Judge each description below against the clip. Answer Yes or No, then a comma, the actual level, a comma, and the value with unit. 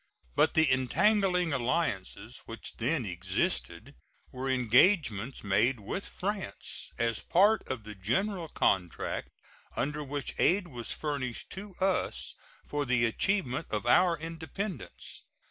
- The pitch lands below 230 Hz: Yes, low, 135 Hz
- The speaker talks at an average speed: No, slow, 125 wpm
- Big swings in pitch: Yes, wide, 7.6 semitones